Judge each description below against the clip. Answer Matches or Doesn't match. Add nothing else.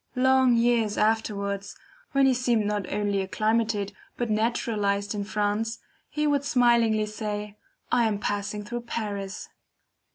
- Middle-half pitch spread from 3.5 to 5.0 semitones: Doesn't match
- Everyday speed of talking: Doesn't match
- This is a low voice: Doesn't match